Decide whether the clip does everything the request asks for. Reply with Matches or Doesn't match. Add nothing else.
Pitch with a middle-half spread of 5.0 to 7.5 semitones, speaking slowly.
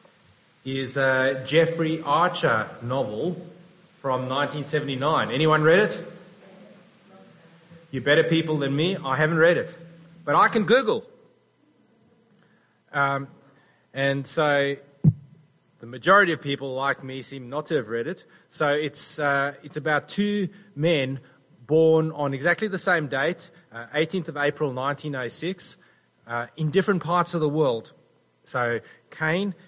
Doesn't match